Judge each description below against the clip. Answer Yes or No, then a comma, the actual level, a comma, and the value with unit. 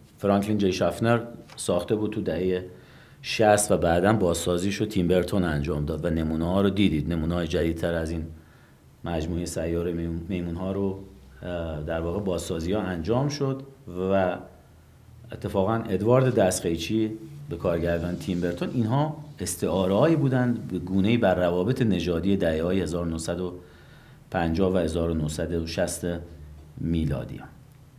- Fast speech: No, average, 125 wpm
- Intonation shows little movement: No, average, 4.2 semitones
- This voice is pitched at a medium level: No, very low, 90 Hz